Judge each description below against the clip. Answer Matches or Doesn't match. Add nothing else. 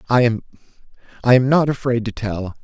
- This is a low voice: Matches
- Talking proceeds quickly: Doesn't match